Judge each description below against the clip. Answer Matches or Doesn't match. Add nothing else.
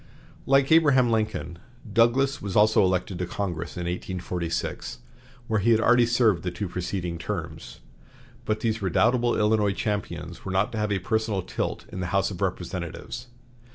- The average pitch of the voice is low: Matches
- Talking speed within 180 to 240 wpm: Doesn't match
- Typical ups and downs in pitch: Matches